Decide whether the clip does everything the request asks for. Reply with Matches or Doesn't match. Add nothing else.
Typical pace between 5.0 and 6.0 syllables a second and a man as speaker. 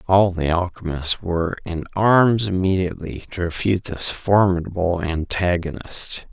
Doesn't match